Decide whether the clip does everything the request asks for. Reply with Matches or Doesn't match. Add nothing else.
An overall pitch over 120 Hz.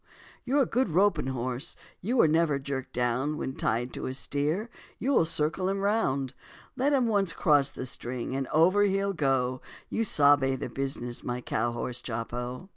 Matches